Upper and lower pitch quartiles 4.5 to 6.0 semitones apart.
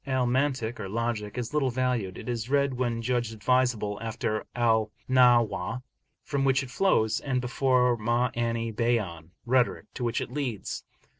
No: narrow, 2.4 semitones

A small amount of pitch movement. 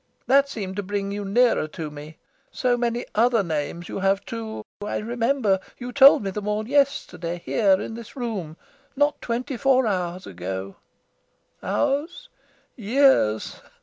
No: average, 5.0 semitones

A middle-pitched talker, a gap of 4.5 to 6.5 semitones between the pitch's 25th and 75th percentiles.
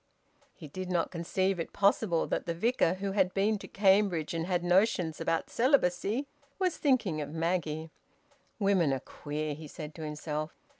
No: medium, 175 Hz; average, 3.9 semitones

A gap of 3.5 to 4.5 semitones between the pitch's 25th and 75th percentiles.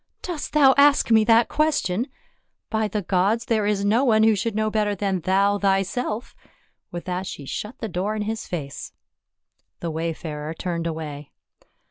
Yes: average, 3.9 semitones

